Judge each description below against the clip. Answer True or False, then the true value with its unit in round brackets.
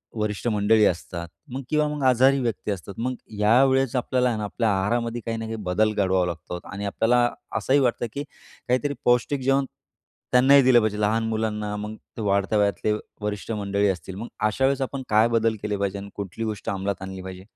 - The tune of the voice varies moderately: True (3.7 semitones)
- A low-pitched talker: True (110 Hz)